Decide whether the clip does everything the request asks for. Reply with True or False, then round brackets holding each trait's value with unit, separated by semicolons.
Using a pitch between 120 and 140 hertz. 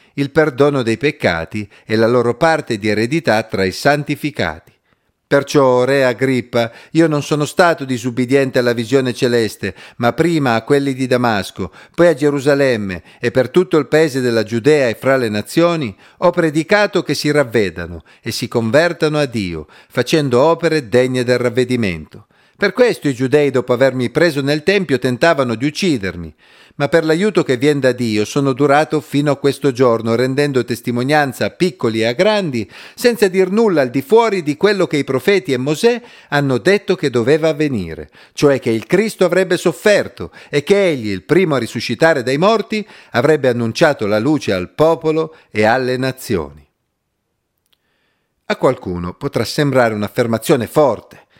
True (135 Hz)